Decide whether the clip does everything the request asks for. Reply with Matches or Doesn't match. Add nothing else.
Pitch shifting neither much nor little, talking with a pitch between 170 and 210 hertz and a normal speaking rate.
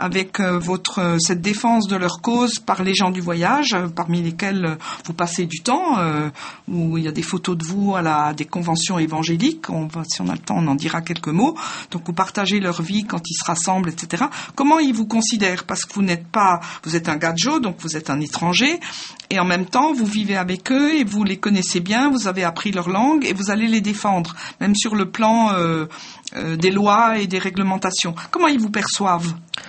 Doesn't match